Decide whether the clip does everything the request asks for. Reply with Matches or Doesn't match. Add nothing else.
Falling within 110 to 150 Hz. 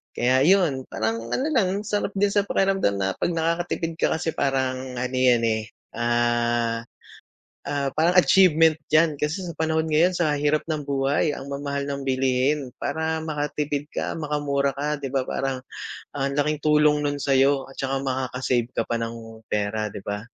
Matches